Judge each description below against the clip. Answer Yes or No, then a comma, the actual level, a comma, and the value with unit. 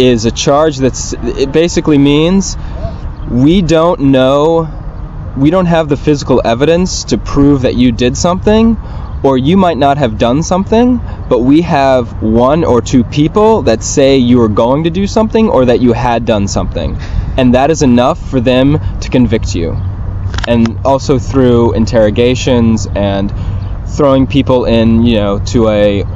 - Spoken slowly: No, average, 165 wpm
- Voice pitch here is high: No, low, 125 Hz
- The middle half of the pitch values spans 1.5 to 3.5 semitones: No, average, 5.2 semitones